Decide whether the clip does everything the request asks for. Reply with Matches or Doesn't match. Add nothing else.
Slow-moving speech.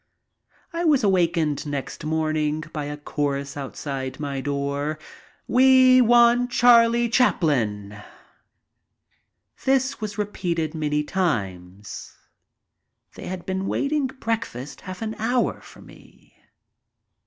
Matches